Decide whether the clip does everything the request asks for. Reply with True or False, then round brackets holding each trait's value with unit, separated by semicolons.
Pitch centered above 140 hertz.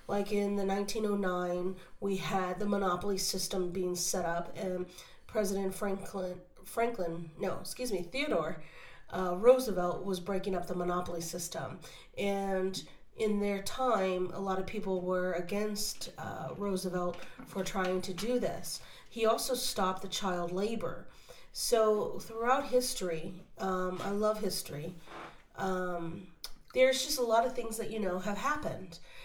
True (190 Hz)